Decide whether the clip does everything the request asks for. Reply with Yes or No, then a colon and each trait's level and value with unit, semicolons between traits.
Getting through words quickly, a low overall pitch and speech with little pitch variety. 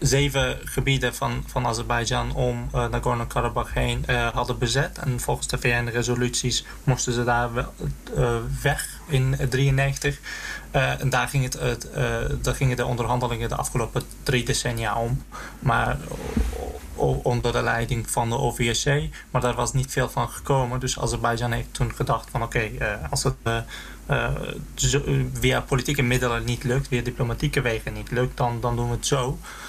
No: average, 170 wpm; low, 125 Hz; narrow, 2.2 semitones